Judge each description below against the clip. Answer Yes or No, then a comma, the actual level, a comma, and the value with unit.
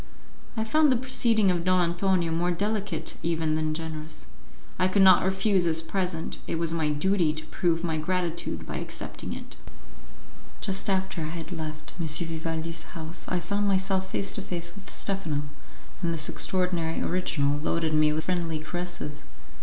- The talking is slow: No, average, 165 wpm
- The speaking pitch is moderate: Yes, medium, 170 Hz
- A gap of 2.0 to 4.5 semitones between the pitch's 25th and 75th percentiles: Yes, average, 2.9 semitones